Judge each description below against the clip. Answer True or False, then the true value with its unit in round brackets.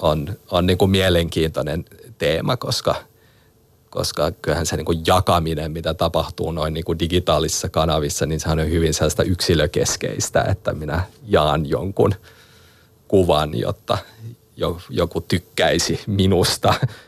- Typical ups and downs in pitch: True (3.5 semitones)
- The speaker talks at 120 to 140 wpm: True (125 wpm)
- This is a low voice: True (85 Hz)